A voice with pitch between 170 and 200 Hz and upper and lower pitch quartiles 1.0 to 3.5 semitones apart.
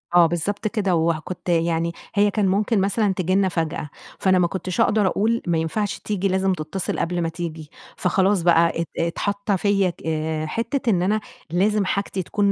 Yes: medium, 185 Hz; average, 3.2 semitones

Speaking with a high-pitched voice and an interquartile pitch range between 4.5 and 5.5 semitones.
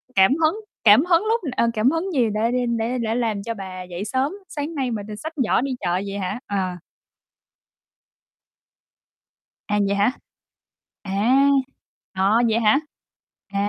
Yes: high, 225 Hz; average, 4.9 semitones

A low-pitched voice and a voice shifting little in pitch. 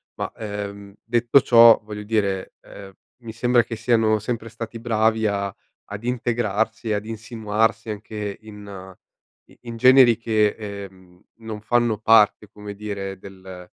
Yes: low, 110 Hz; narrow, 2.1 semitones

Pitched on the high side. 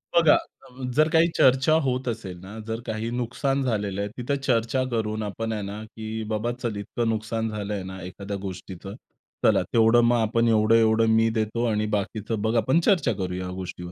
No: low, 110 Hz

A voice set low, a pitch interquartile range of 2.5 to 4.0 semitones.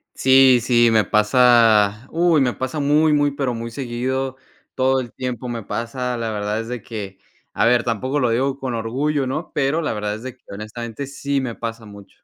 Yes: low, 125 Hz; average, 2.9 semitones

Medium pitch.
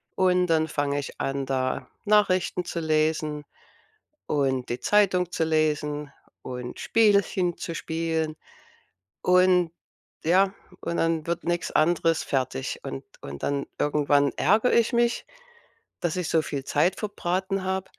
Yes: medium, 165 Hz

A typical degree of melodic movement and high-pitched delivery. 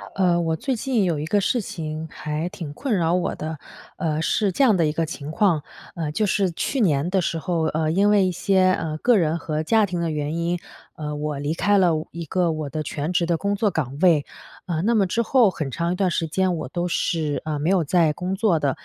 No: average, 3.6 semitones; medium, 170 Hz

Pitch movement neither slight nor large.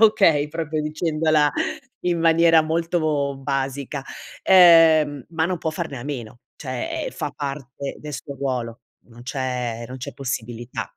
Yes: average, 3.7 semitones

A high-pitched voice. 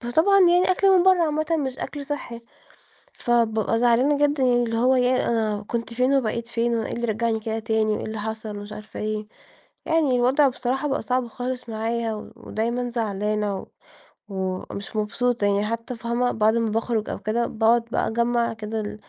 Yes: high, 235 Hz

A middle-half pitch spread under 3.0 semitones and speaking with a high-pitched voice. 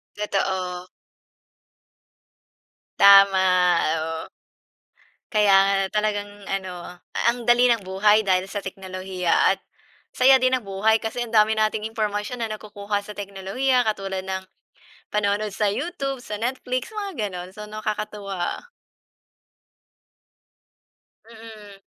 Yes: narrow, 2.5 semitones; high, 210 Hz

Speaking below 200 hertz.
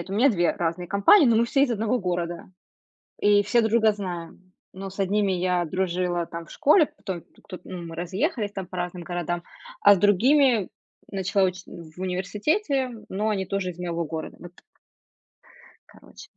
Yes: high, 190 Hz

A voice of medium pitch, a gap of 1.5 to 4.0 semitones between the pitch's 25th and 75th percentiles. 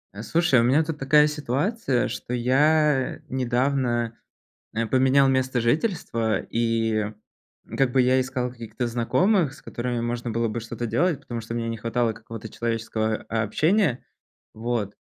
No: low, 120 Hz; average, 3.0 semitones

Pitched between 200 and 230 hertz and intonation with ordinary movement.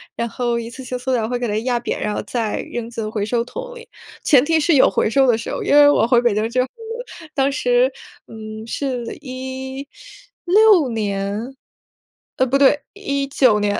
No: very high, 250 Hz; average, 3.6 semitones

